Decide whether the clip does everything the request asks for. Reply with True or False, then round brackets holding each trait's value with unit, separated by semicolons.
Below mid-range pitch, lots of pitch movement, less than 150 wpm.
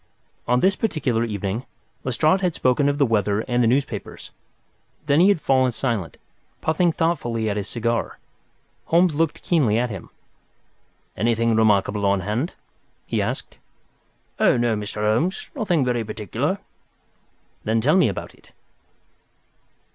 True (120 Hz; 6.0 semitones; 135 wpm)